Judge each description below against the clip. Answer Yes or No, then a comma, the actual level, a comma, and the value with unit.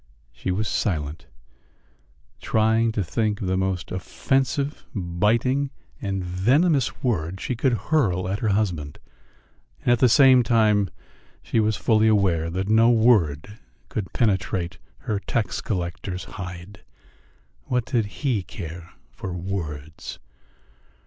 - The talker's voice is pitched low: Yes, low, 100 Hz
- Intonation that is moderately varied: Yes, average, 4.3 semitones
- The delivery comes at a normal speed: No, slow, 125 wpm